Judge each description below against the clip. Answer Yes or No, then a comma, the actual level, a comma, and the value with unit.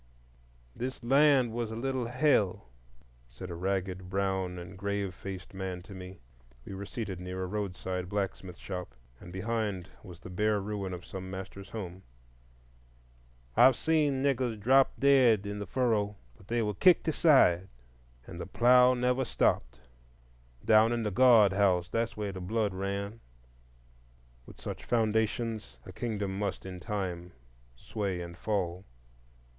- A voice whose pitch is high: No, low, 100 Hz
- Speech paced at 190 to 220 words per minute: No, average, 150 wpm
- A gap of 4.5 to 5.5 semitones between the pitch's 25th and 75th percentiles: No, average, 3.9 semitones